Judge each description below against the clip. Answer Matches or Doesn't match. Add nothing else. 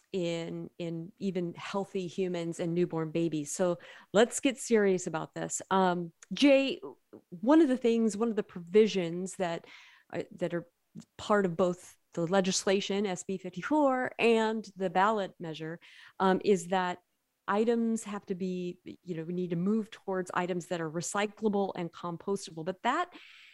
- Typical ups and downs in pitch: Matches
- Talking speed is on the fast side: Doesn't match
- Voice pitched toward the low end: Doesn't match